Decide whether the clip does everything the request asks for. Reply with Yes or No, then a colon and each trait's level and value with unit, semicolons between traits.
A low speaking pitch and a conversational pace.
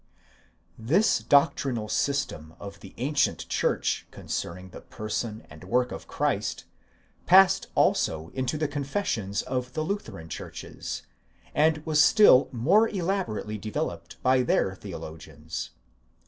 No: low, 125 Hz; slow, 120 wpm